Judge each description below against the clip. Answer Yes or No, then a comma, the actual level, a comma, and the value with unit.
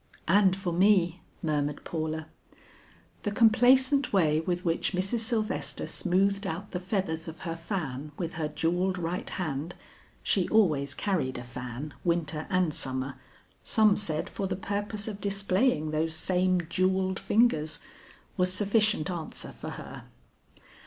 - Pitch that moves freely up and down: No, average, 4.0 semitones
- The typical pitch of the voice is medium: Yes, medium, 180 Hz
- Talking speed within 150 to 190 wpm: No, average, 140 wpm